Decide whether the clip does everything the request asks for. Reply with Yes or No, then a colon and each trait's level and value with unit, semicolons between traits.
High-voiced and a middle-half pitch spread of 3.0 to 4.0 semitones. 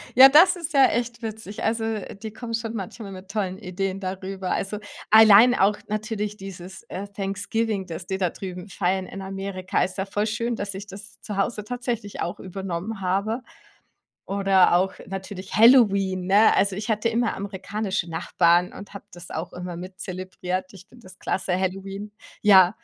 No: high, 195 Hz; narrow, 2.5 semitones